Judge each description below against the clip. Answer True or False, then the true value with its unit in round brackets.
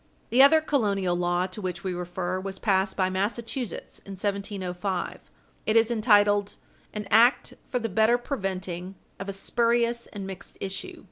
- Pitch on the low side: False (200 Hz)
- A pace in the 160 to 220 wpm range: True (175 wpm)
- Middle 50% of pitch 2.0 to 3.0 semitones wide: False (3.6 semitones)